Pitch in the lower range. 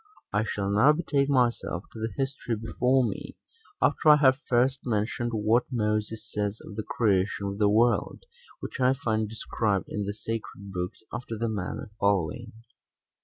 Yes: low, 110 Hz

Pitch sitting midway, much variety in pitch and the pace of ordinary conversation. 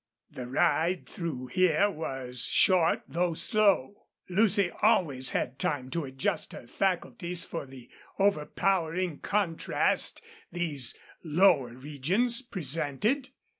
No: medium, 165 Hz; wide, 6.0 semitones; slow, 105 wpm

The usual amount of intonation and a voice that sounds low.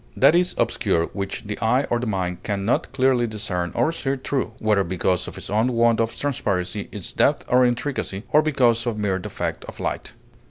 Yes: average, 4.5 semitones; low, 115 Hz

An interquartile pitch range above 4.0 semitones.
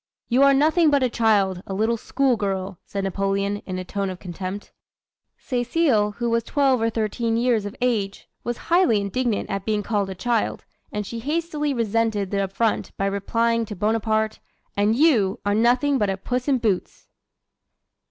No: average, 3.7 semitones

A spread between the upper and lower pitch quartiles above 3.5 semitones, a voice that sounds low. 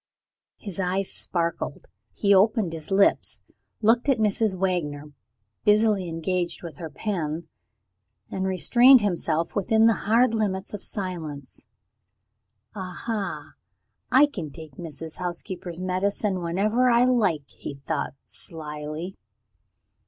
No: average, 4.4 semitones; medium, 185 Hz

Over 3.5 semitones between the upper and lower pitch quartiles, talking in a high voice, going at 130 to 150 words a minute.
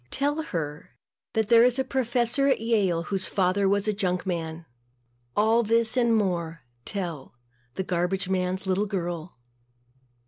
Yes: average, 4.4 semitones; high, 195 Hz; average, 145 wpm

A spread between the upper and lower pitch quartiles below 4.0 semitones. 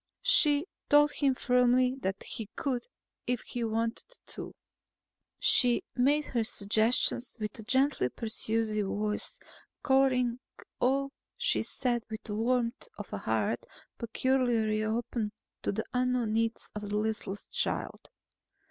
Yes: average, 2.9 semitones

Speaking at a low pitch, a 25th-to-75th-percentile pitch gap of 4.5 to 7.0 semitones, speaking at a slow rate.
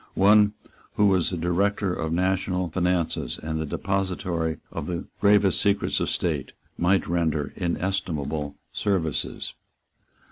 No: very low, 90 Hz; average, 3.1 semitones; slow, 130 wpm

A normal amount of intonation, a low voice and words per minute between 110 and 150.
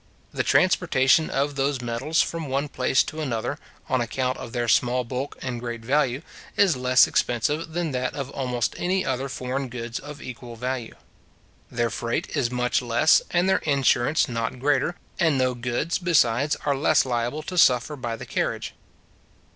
No: average, 3.3 semitones; low, 130 Hz; average, 170 wpm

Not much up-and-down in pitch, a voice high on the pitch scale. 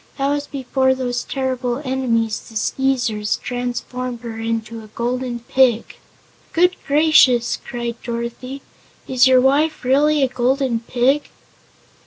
Yes: narrow, 2.2 semitones; very high, 250 Hz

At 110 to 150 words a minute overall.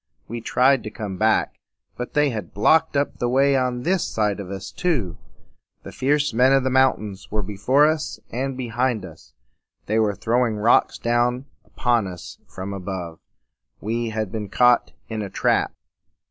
No: average, 175 wpm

